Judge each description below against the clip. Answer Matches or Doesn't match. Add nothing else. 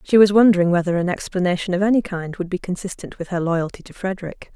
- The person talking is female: Matches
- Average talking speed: Doesn't match